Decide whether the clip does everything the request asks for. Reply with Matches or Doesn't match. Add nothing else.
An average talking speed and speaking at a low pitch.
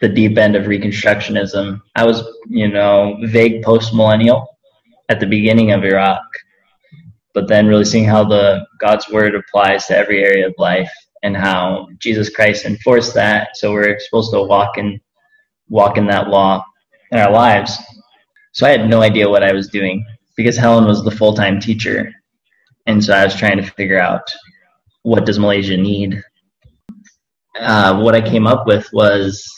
Matches